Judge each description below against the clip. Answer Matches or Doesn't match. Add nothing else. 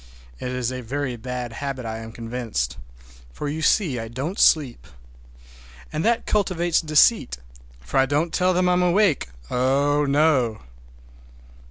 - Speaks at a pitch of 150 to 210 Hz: Doesn't match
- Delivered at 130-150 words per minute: Matches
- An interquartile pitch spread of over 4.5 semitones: Matches